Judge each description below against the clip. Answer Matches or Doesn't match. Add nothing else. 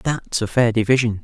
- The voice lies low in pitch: Matches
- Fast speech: Doesn't match